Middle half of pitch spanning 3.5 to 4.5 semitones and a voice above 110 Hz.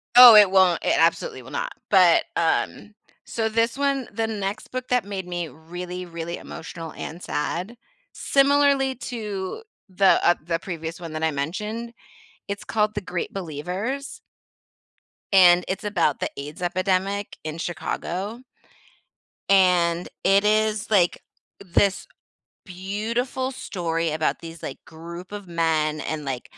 Yes: average, 4.1 semitones; medium, 185 Hz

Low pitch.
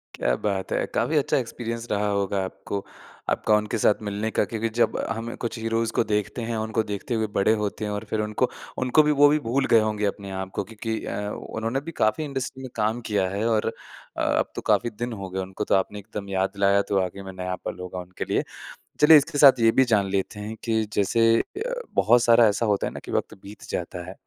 Yes: low, 110 Hz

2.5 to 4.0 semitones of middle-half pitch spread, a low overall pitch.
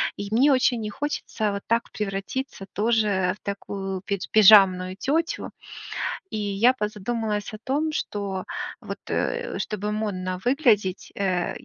No: average, 3.2 semitones; high, 210 Hz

